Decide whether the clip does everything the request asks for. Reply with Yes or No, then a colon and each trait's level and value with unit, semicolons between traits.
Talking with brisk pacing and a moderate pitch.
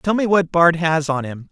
Yes: fast, 275 wpm; medium, 165 Hz